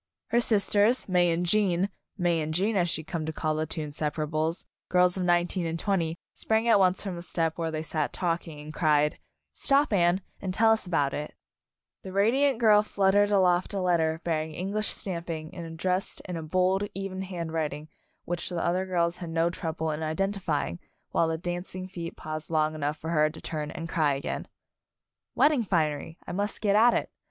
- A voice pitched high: No, medium, 175 Hz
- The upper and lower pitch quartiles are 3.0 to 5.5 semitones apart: Yes, average, 3.3 semitones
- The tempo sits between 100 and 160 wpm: No, average, 200 wpm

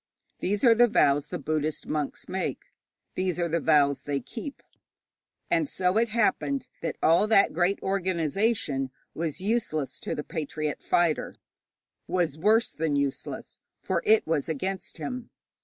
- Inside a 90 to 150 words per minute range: Yes, average, 145 wpm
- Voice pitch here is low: No, medium, 175 Hz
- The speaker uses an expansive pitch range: Yes, wide, 6.0 semitones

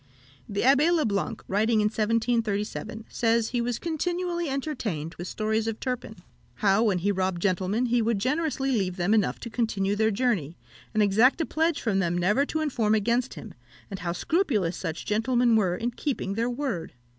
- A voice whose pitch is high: Yes, high, 225 Hz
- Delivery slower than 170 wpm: No, average, 180 wpm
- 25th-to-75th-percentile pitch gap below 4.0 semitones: No, average, 4.3 semitones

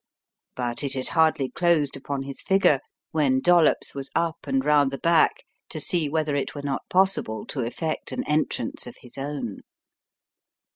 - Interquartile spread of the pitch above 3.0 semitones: Yes, average, 3.4 semitones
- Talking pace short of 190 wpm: Yes, average, 165 wpm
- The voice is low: No, medium, 145 Hz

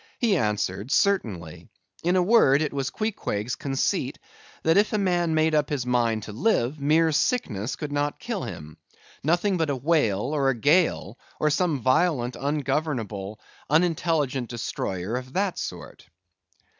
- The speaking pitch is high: No, medium, 145 Hz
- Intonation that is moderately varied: No, wide, 5.8 semitones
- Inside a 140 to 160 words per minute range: Yes, average, 150 wpm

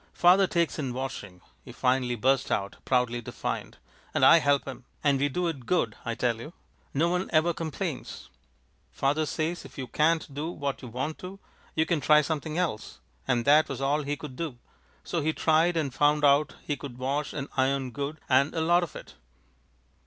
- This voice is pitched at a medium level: Yes, medium, 145 Hz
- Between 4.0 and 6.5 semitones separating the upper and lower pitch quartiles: No, average, 3.4 semitones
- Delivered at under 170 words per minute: No, average, 195 wpm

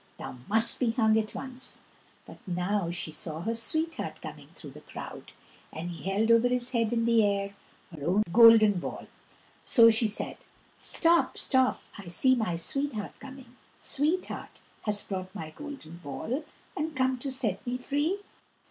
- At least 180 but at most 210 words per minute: No, average, 165 wpm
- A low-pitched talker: No, high, 230 Hz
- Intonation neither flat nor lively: Yes, average, 4.9 semitones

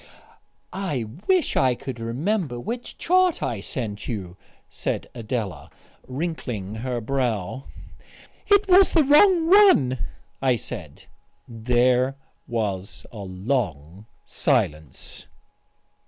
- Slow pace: Yes, slow, 100 wpm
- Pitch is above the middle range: No, low, 125 Hz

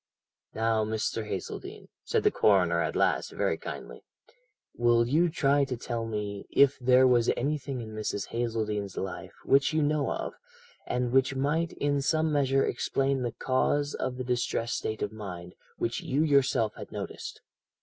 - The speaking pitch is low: Yes, low, 125 Hz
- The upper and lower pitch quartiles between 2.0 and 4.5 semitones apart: Yes, average, 4.1 semitones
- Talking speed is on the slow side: No, average, 160 wpm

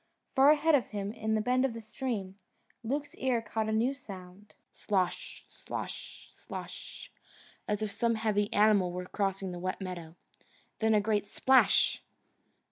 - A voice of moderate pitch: No, high, 215 Hz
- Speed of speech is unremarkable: Yes, average, 155 wpm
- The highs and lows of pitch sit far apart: No, average, 3.3 semitones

